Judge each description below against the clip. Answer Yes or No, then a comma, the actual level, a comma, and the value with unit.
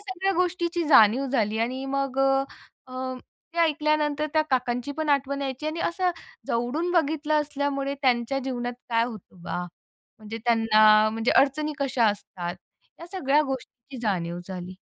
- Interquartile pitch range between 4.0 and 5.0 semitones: Yes, average, 4.5 semitones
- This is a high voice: Yes, very high, 270 Hz